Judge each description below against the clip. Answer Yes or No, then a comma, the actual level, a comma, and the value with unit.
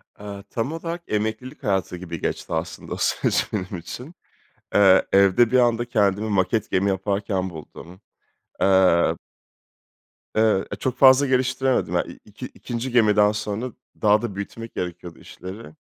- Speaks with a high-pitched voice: No, low, 105 Hz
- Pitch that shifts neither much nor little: Yes, average, 4.1 semitones